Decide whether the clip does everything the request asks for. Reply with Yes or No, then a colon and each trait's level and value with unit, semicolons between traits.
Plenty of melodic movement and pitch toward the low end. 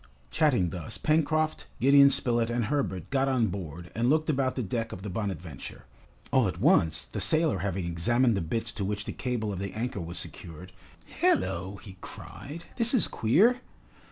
Yes: wide, 6.9 semitones; low, 115 Hz